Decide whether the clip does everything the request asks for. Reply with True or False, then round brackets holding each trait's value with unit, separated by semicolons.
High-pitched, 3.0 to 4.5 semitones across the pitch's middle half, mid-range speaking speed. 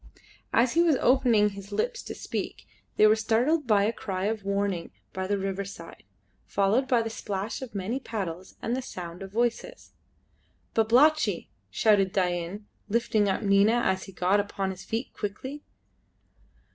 True (205 Hz; 3.4 semitones; 160 wpm)